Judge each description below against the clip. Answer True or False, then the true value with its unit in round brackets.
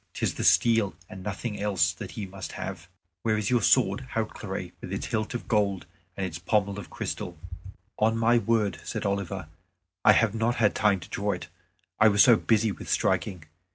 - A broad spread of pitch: False (2.8 semitones)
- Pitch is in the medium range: False (105 Hz)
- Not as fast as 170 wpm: False (190 wpm)